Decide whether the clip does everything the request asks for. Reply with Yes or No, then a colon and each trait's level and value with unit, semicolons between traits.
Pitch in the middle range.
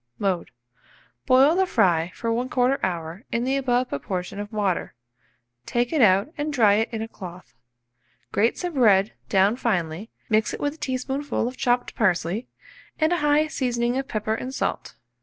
No: high, 230 Hz